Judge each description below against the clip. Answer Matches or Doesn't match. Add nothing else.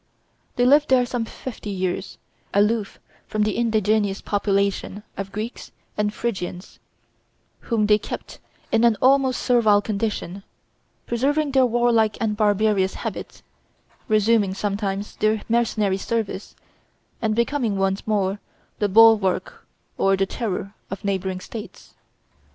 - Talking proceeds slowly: Matches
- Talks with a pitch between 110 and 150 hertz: Doesn't match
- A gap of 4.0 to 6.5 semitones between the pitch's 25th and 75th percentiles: Doesn't match